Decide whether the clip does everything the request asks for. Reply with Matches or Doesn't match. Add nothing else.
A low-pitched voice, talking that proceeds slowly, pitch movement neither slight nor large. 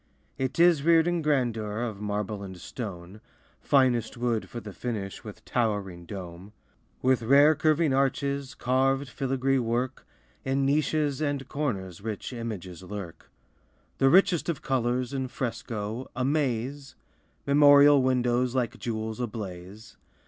Matches